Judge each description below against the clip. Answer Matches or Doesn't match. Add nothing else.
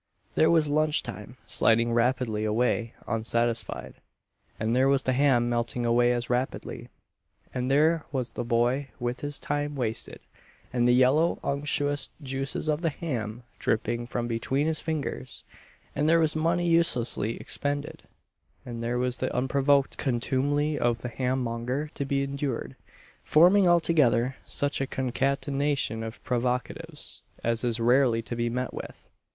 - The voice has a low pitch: Matches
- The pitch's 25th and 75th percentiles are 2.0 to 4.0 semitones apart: Matches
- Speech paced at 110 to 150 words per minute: Matches